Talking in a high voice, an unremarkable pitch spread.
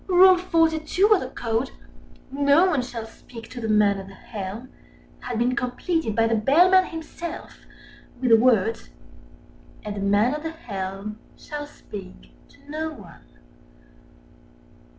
No: very high, 250 Hz; wide, 6.9 semitones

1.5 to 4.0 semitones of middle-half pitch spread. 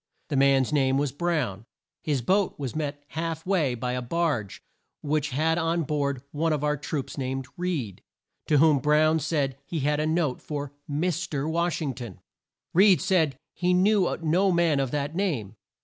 Yes: average, 3.5 semitones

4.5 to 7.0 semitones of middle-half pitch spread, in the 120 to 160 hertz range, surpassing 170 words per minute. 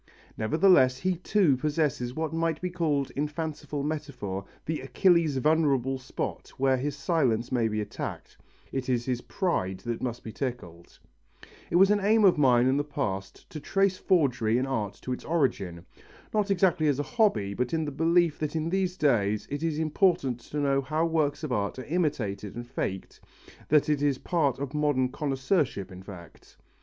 Yes: average, 4.8 semitones; medium, 140 Hz; average, 180 wpm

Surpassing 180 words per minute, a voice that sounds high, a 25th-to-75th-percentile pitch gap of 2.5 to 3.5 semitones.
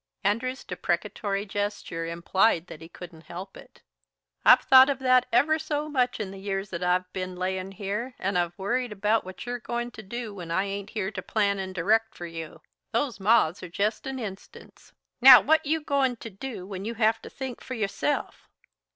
No: average, 195 wpm; high, 205 Hz; average, 4.7 semitones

